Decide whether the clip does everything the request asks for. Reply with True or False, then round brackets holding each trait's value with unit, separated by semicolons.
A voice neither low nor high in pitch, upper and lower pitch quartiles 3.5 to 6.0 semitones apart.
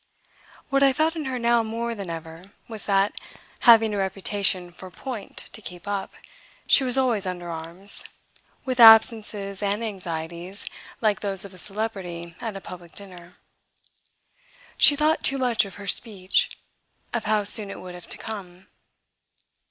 False (200 Hz; 3.9 semitones)